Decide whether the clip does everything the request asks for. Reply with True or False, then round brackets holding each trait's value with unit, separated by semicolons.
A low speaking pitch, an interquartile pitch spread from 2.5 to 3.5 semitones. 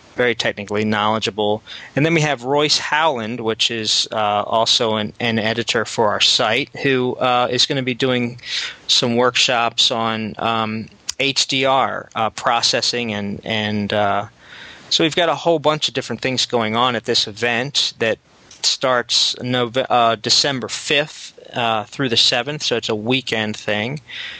True (120 Hz; 3.0 semitones)